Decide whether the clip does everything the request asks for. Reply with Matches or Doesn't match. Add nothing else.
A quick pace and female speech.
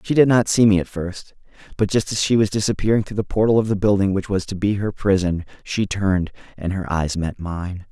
Doesn't match